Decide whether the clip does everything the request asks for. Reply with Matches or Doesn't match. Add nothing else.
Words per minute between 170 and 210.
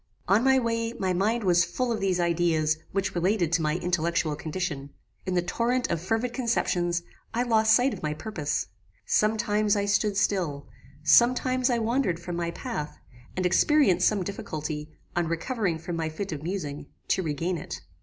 Matches